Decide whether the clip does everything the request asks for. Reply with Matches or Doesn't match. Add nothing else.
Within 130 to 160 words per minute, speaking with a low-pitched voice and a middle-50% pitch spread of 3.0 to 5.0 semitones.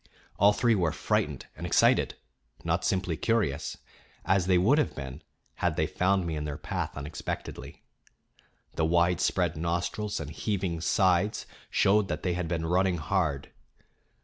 Matches